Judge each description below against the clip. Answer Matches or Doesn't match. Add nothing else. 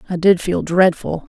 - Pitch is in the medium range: Matches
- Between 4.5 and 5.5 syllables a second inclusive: Matches